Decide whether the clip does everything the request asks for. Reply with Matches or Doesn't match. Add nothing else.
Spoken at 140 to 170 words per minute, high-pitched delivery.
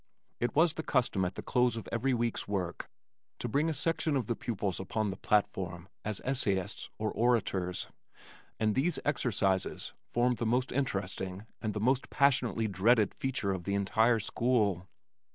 Doesn't match